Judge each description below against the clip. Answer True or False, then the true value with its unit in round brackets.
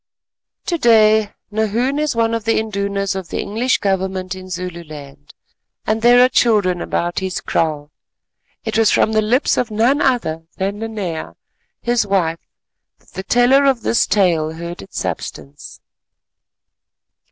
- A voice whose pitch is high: True (205 Hz)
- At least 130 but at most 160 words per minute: True (145 wpm)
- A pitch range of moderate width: True (4.4 semitones)